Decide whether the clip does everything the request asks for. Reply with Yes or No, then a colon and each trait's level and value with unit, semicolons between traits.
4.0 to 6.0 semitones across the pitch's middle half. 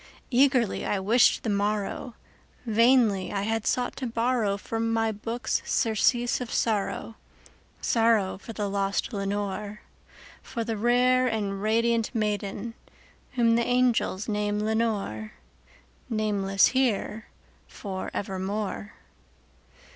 No: narrow, 2.6 semitones